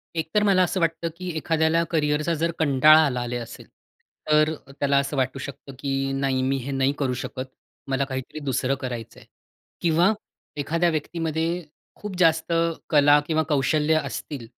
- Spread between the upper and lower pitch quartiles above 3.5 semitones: No, average, 3.2 semitones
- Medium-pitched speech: Yes, medium, 150 Hz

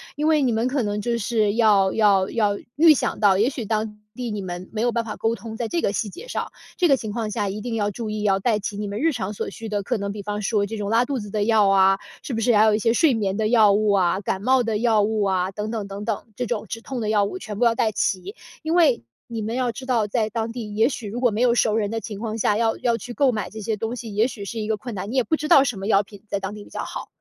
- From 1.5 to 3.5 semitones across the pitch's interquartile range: Yes, narrow, 2.6 semitones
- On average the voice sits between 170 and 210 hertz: No, high, 220 Hz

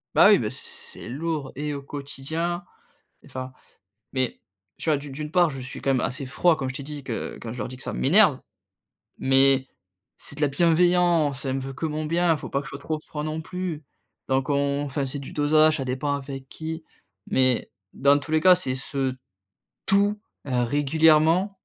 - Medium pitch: Yes, medium, 145 Hz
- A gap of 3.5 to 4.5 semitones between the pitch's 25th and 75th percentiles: No, average, 3.0 semitones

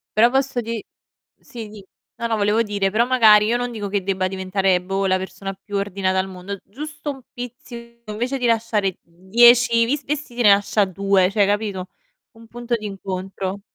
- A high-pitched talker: Yes, high, 210 Hz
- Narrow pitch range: No, average, 3.4 semitones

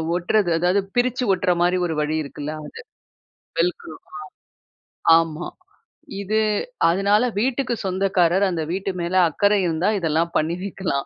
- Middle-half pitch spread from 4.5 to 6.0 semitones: No, average, 3.3 semitones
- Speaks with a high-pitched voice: No, medium, 180 Hz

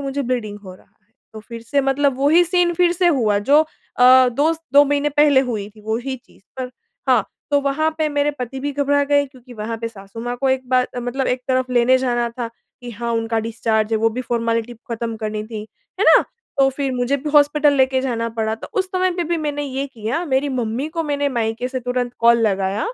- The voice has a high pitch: Yes, very high, 255 Hz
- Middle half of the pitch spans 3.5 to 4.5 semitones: Yes, average, 3.8 semitones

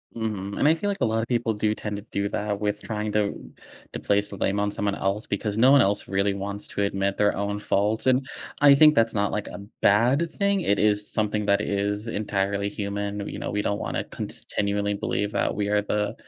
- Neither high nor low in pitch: No, low, 105 Hz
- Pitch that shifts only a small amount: Yes, narrow, 1.6 semitones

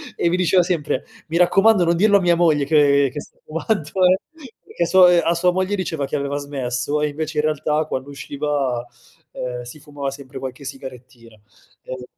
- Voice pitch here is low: No, medium, 150 Hz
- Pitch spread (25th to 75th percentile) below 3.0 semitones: No, average, 4.1 semitones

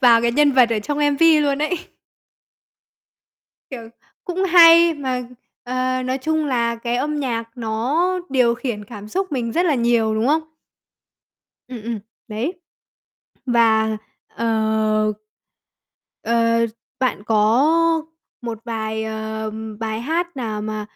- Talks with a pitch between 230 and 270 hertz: Yes, high, 235 Hz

